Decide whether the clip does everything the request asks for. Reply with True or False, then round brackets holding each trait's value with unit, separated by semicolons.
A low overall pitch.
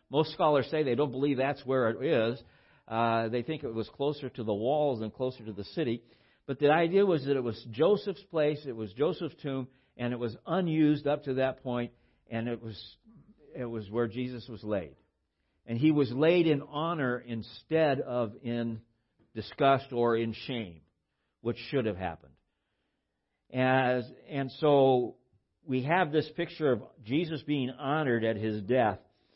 True (125 Hz)